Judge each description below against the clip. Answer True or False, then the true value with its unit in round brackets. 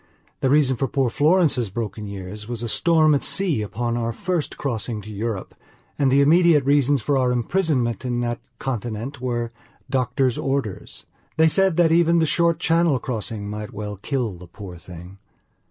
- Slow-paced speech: False (170 wpm)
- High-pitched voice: False (125 Hz)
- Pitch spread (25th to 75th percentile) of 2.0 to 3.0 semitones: False (5.3 semitones)